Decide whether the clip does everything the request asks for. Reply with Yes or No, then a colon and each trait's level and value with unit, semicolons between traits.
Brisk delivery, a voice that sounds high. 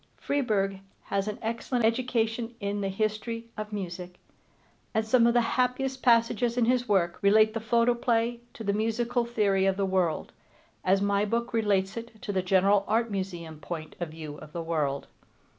No: average, 175 wpm; high, 215 Hz